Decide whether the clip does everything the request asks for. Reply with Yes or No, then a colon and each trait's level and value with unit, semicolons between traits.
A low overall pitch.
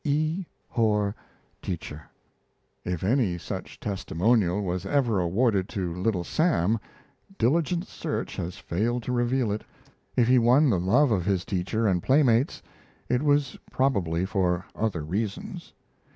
Yes: low, 105 Hz